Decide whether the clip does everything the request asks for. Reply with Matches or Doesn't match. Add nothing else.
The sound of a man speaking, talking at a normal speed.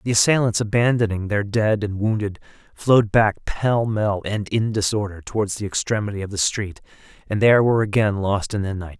Matches